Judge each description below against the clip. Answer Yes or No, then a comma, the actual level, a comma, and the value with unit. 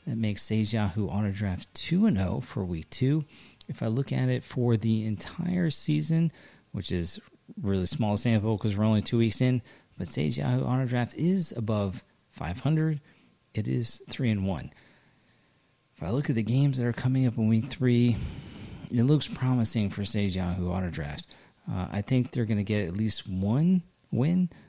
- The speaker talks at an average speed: Yes, average, 180 wpm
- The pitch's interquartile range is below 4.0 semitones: No, average, 4.3 semitones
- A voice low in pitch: Yes, low, 115 Hz